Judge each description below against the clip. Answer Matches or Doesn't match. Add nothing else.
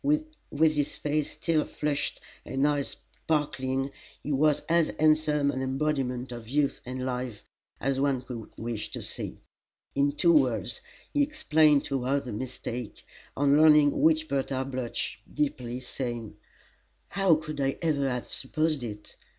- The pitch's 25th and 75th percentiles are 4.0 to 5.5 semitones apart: Doesn't match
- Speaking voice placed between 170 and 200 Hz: Doesn't match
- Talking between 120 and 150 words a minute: Matches